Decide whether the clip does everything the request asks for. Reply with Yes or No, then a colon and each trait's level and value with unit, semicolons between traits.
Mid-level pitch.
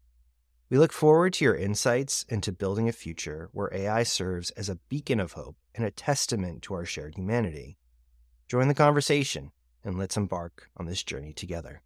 No: very low, 95 Hz